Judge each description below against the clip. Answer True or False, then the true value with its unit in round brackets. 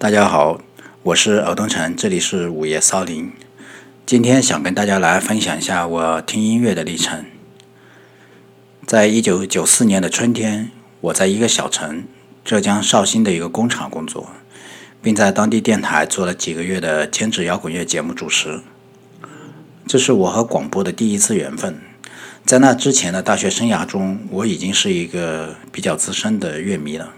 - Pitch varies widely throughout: False (5.0 semitones)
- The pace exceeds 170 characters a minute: True (255 characters per minute)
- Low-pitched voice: True (100 Hz)